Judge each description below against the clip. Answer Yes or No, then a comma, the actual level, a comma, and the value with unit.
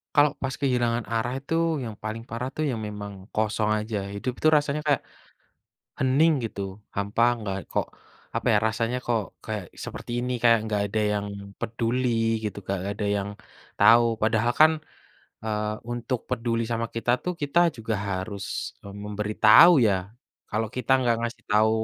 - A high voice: No, low, 115 Hz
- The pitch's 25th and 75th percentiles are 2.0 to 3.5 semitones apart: Yes, average, 3.0 semitones